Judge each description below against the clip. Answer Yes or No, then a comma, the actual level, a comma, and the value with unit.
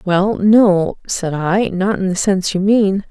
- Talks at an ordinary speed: Yes, average, 195 wpm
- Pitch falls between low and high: No, high, 195 Hz